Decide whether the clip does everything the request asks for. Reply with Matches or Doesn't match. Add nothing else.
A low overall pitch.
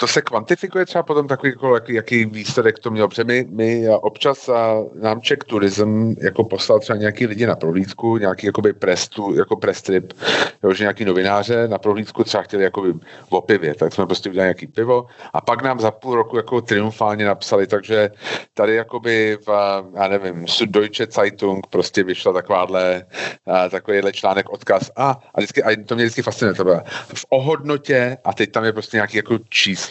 Matches